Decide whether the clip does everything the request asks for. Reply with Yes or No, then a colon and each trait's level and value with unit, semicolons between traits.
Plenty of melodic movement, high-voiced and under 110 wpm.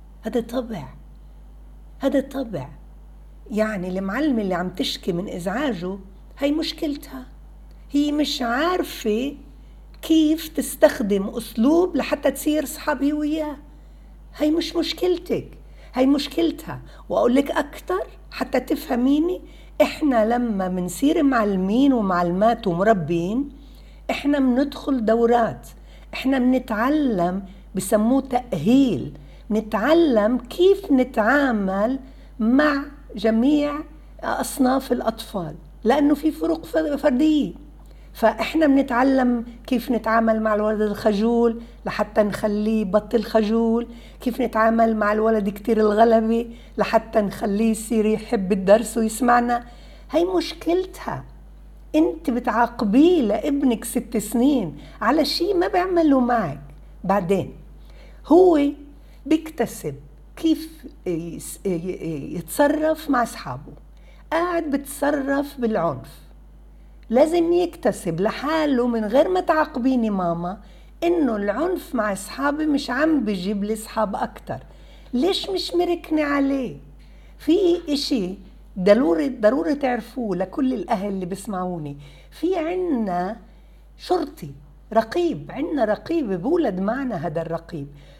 Yes: wide, 5.7 semitones; high, 240 Hz; average, 95 wpm